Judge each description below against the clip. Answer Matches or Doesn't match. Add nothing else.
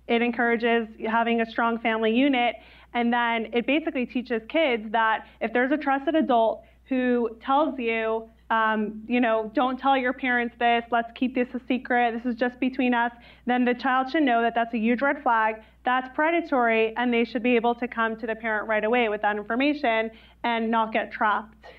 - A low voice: Doesn't match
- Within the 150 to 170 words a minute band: Doesn't match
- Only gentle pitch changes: Matches